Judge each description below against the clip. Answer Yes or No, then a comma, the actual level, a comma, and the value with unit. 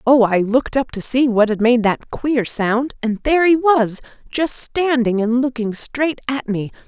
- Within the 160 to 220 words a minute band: Yes, average, 200 wpm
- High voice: Yes, high, 245 Hz